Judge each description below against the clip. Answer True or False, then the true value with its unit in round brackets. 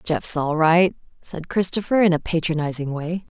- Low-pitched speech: False (165 Hz)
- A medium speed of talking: True (160 wpm)